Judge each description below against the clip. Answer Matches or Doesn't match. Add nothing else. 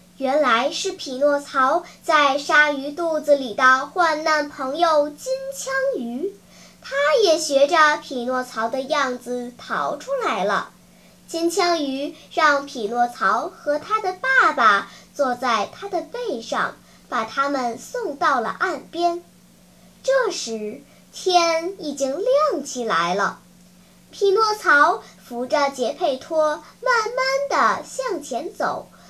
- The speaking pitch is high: Matches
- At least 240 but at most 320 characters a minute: Doesn't match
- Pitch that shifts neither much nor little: Matches